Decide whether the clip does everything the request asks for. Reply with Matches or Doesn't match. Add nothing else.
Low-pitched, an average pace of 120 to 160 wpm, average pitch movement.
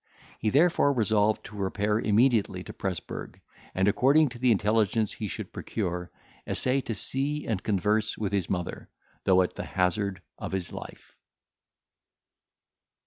Matches